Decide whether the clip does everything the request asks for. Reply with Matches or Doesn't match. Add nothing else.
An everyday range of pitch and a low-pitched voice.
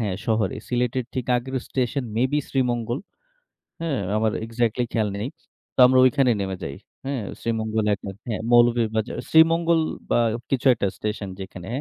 Matches